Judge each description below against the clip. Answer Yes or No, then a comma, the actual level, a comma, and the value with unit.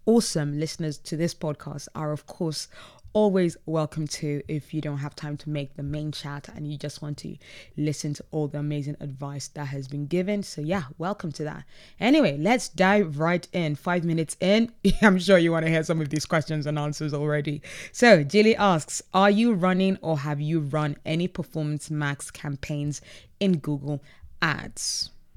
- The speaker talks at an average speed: Yes, average, 185 wpm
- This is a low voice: No, medium, 155 Hz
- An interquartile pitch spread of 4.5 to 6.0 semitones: No, average, 3.5 semitones